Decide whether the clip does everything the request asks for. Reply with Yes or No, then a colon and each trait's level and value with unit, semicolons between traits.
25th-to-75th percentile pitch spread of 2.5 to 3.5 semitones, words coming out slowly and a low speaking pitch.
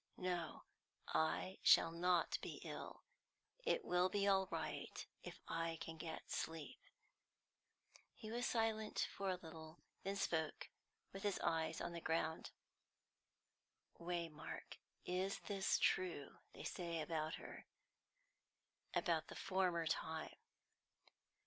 No: average, 3.0 semitones; slow, 115 wpm; medium, 170 Hz